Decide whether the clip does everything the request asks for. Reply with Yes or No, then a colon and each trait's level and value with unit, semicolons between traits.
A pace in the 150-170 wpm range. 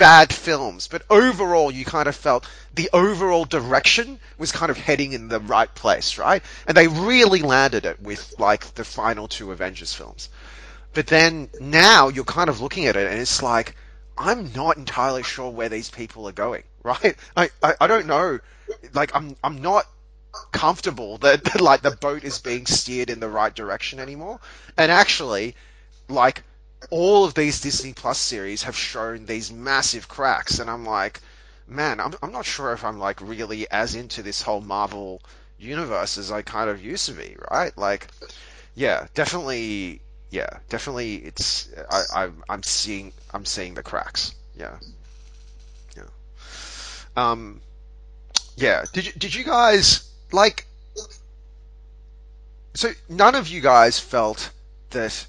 Yes: average, 160 wpm